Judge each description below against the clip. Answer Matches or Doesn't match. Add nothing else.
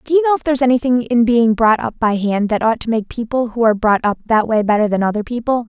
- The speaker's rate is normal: Doesn't match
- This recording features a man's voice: Doesn't match